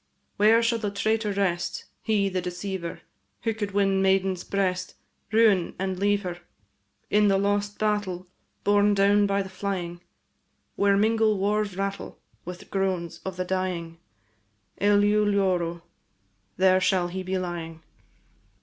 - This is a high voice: Yes, high, 195 Hz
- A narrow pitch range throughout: Yes, narrow, 2.0 semitones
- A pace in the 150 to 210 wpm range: No, average, 140 wpm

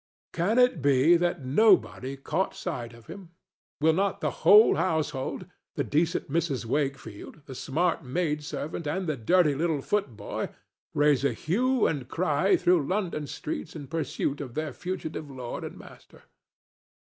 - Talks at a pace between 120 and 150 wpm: Yes, average, 145 wpm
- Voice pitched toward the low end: No, medium, 155 Hz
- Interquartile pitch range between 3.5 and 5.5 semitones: Yes, average, 4.5 semitones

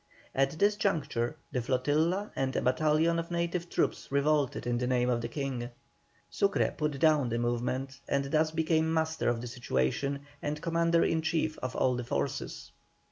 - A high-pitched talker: No, medium, 145 Hz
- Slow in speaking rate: No, average, 175 wpm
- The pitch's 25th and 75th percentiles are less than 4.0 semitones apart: No, average, 4.3 semitones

